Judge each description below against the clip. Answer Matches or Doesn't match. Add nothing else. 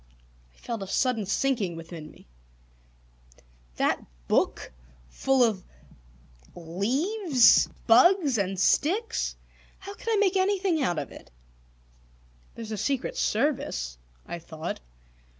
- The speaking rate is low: Matches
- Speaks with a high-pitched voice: Matches